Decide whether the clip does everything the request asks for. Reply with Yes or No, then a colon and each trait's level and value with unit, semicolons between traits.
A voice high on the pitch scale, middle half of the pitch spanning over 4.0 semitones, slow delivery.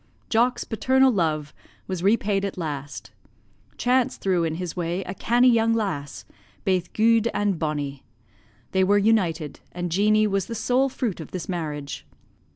No: high, 195 Hz; average, 5.3 semitones; average, 155 wpm